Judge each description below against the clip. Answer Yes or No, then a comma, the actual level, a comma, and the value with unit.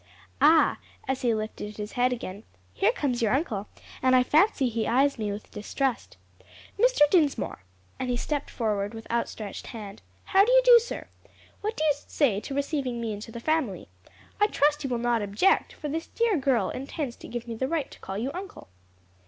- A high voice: Yes, very high, 255 Hz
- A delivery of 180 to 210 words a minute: Yes, average, 195 wpm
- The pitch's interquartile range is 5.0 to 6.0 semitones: Yes, wide, 5.5 semitones